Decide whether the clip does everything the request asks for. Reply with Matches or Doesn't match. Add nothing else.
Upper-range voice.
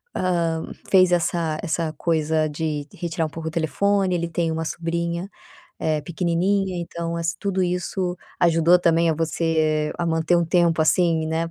Doesn't match